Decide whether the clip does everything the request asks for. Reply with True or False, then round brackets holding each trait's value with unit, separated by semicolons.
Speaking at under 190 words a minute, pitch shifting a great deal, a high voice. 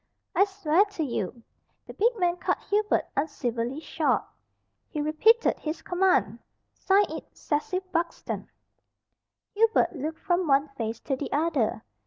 True (140 wpm; 5.7 semitones; 320 Hz)